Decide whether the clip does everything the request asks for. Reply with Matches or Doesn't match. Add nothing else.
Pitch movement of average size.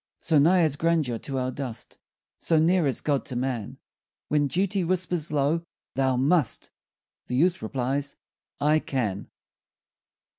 Matches